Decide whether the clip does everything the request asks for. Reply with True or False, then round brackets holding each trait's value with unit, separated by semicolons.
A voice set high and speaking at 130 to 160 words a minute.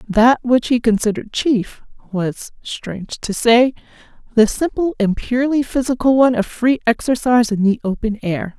True (235 Hz; 155 wpm)